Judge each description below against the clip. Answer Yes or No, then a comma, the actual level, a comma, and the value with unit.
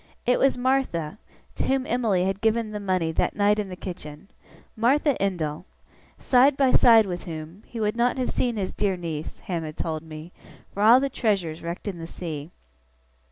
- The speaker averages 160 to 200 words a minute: Yes, average, 190 wpm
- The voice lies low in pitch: No, high, 195 Hz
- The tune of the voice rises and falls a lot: Yes, wide, 6.0 semitones